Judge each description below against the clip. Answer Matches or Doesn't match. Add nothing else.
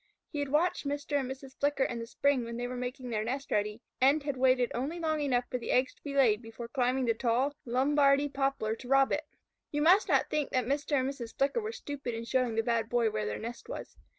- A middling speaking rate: Doesn't match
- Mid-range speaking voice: Doesn't match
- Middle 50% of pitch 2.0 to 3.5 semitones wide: Matches